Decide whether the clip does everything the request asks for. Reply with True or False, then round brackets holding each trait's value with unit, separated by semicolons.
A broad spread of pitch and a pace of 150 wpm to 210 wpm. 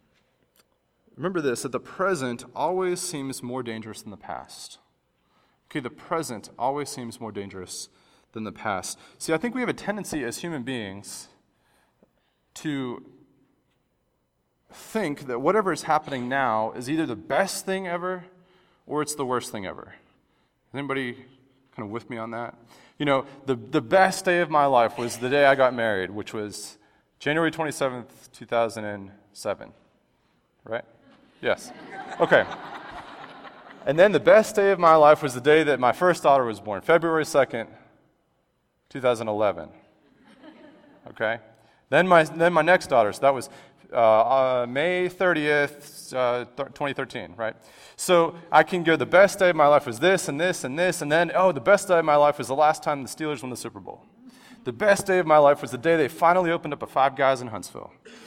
True (6.0 semitones; 180 wpm)